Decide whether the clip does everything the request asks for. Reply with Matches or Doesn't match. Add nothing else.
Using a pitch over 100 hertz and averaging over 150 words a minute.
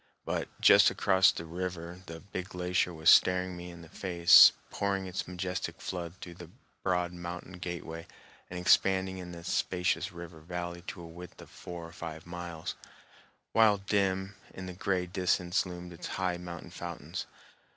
Doesn't match